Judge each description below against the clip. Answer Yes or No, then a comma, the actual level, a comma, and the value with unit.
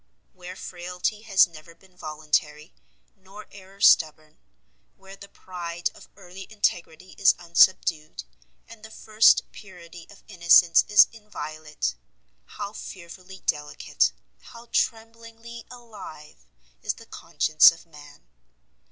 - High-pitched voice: No, medium, 180 Hz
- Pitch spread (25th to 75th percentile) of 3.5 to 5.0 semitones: Yes, average, 4.3 semitones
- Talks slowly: Yes, slow, 115 wpm